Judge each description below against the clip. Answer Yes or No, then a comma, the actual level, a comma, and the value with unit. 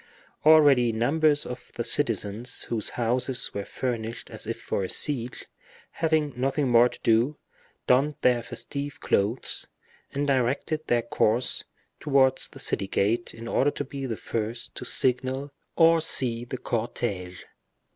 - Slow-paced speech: No, average, 145 wpm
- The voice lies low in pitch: Yes, low, 125 Hz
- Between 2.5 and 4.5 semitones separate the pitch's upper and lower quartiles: Yes, average, 3.4 semitones